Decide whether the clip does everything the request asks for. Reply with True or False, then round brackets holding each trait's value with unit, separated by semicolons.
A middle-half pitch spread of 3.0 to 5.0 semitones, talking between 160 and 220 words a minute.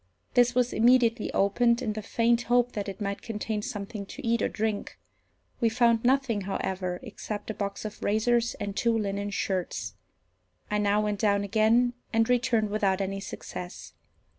False (2.6 semitones; 165 wpm)